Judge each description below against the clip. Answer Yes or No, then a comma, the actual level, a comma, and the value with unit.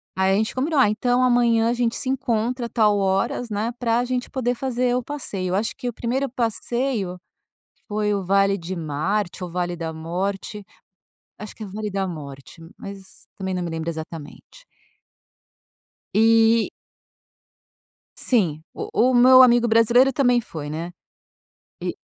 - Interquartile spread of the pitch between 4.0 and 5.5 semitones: Yes, average, 4.6 semitones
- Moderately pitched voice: No, high, 215 Hz